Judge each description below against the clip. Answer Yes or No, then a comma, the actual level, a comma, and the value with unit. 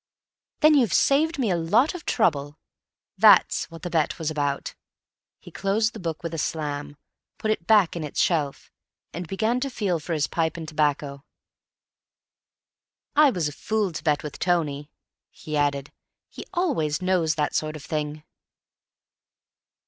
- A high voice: No, medium, 165 Hz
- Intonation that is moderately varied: No, wide, 5.9 semitones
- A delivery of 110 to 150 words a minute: No, average, 160 wpm